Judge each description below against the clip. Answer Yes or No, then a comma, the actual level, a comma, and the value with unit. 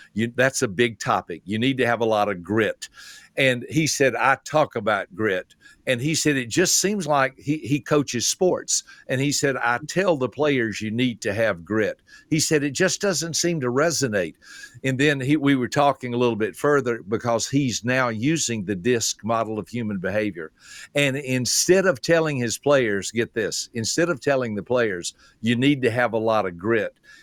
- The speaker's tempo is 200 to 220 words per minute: Yes, fast, 205 wpm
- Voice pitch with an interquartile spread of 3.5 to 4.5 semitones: Yes, average, 4.1 semitones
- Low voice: Yes, low, 130 Hz